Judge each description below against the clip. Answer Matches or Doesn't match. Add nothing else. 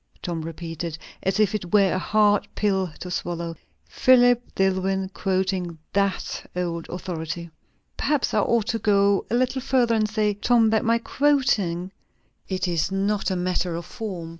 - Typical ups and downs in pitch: Matches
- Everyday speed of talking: Matches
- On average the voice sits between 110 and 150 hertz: Doesn't match